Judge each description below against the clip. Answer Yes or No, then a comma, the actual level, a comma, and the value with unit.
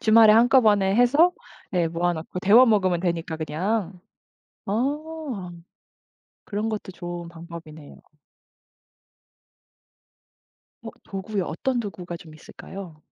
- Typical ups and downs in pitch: Yes, average, 4.7 semitones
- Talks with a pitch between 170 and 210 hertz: Yes, high, 190 Hz